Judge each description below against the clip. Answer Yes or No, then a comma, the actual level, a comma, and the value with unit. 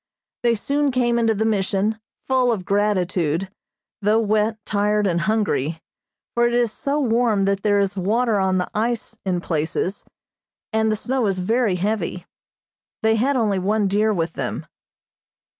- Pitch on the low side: No, high, 210 Hz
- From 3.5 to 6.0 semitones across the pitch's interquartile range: No, average, 3.1 semitones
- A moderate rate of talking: Yes, average, 160 wpm